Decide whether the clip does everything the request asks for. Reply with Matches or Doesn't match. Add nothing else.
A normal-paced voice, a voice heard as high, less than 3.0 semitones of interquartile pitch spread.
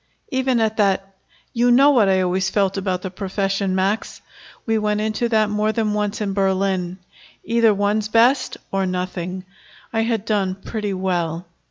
Matches